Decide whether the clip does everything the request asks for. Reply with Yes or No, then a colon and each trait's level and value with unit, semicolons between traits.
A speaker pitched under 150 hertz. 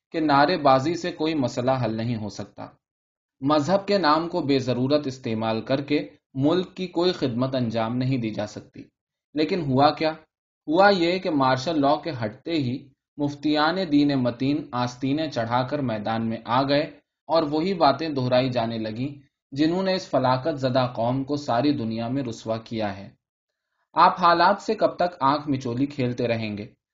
Yes: medium, 140 Hz